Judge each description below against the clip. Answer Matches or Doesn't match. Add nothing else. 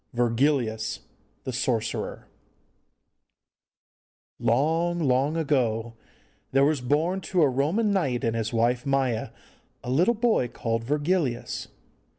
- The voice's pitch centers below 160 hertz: Matches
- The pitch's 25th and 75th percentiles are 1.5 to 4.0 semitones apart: Doesn't match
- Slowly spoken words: Matches